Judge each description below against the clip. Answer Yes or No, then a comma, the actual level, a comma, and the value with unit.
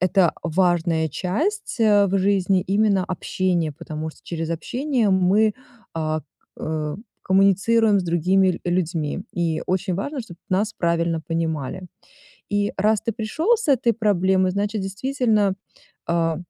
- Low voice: No, high, 190 Hz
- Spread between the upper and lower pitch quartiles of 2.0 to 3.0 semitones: No, average, 3.8 semitones